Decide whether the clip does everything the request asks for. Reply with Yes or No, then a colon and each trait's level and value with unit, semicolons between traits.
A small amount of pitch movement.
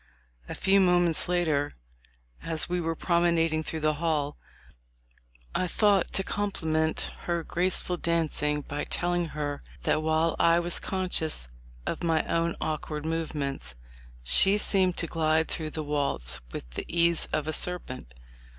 Yes: narrow, 2.3 semitones